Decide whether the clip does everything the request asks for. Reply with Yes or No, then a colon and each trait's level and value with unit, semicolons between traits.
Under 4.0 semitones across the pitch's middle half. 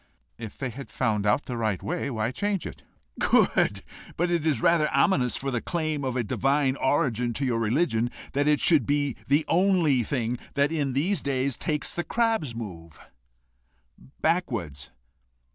No: average, 4.9 semitones